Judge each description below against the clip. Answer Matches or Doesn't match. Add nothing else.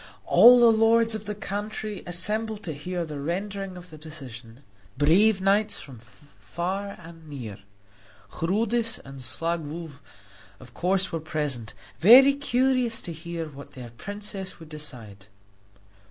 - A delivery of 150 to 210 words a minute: Doesn't match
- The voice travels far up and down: Matches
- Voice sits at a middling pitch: Matches